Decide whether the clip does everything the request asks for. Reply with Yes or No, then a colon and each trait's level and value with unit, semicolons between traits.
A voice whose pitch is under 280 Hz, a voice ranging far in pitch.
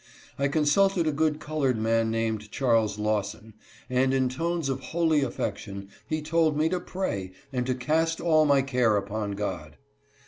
Yes: low, 135 Hz; wide, 6.2 semitones